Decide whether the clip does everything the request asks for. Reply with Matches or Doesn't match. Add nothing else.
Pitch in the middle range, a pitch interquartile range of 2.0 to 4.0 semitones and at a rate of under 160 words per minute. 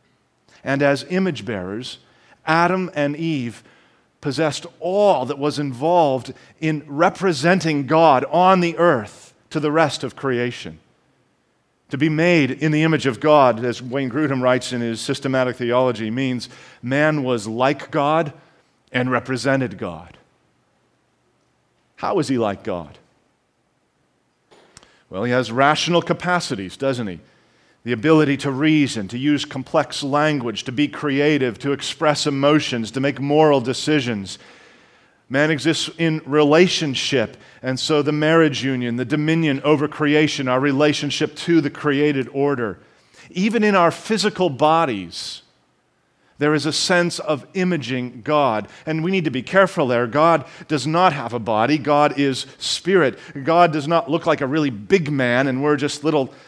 Matches